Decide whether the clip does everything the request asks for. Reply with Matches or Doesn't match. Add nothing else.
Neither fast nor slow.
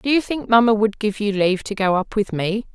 Doesn't match